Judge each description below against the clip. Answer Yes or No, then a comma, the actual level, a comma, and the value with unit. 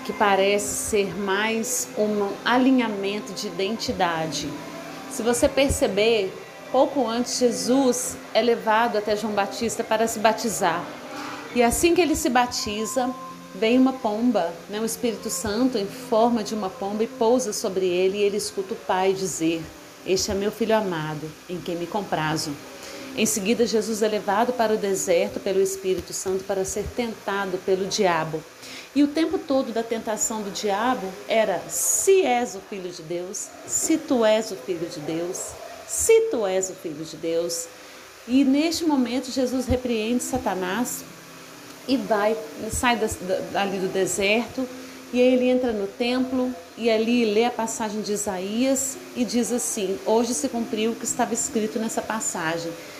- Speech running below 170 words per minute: Yes, average, 160 wpm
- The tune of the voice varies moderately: Yes, average, 4.1 semitones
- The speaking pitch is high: Yes, high, 220 Hz